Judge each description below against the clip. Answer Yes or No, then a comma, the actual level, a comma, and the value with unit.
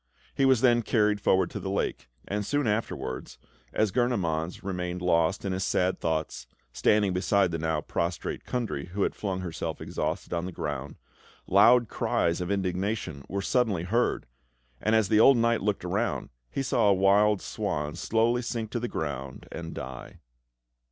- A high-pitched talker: No, very low, 95 Hz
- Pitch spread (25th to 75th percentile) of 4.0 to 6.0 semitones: Yes, average, 4.7 semitones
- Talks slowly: No, average, 170 wpm